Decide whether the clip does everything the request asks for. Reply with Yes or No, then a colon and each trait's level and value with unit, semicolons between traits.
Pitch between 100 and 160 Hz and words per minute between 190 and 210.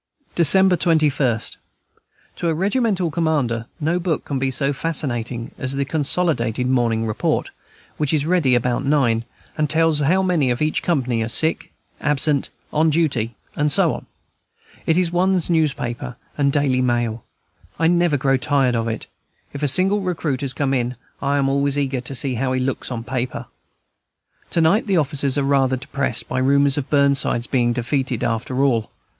No: medium, 140 Hz; average, 170 wpm